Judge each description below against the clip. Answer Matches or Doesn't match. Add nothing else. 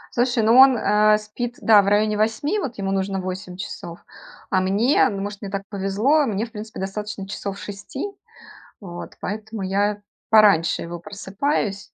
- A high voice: Matches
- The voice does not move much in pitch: Matches